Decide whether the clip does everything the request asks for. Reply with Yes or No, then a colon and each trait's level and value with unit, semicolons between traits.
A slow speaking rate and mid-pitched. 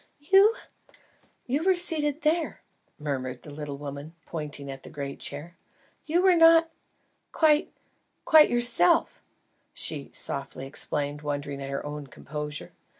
Yes: slow, 130 wpm; medium, 150 Hz